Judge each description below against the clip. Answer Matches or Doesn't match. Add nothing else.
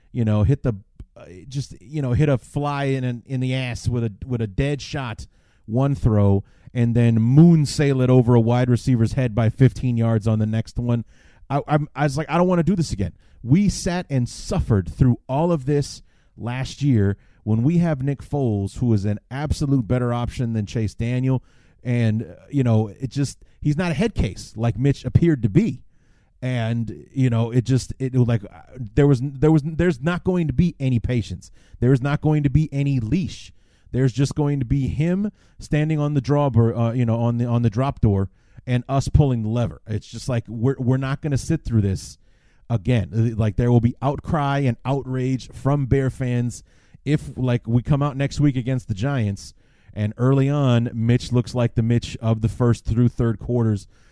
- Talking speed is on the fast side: Matches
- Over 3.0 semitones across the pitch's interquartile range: Matches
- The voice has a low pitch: Matches